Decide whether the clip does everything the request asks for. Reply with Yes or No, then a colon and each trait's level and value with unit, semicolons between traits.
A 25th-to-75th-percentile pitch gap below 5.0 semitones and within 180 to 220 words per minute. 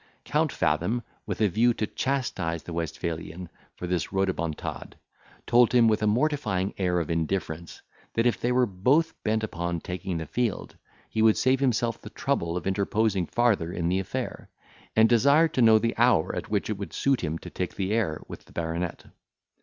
No: wide, 5.4 semitones; average, 185 wpm